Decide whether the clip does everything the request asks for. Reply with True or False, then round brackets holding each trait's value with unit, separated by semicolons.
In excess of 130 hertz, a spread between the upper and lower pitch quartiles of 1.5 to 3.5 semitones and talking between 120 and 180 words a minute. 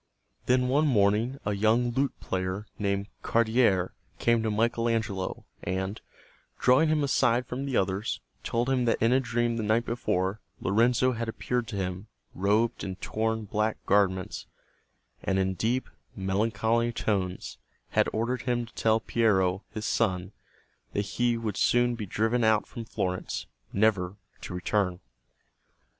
False (110 Hz; 3.2 semitones; 150 wpm)